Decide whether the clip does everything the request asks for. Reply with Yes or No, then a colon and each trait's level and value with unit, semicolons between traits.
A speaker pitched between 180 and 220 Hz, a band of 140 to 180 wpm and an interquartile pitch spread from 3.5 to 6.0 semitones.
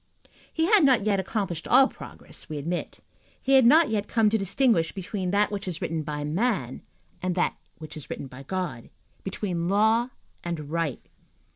Yes: high, 190 Hz; average, 175 wpm; average, 5.3 semitones